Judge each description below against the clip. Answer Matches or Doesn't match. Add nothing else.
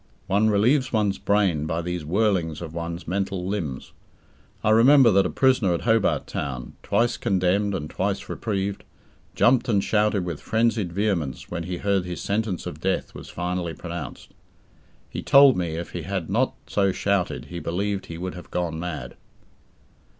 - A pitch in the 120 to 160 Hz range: Doesn't match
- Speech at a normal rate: Matches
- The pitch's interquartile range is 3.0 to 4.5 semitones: Matches